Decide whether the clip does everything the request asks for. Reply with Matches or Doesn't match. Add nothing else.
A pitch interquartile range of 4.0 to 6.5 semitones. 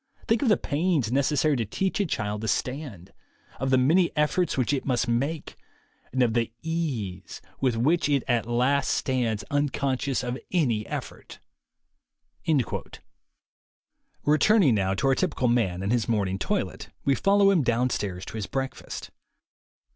Matches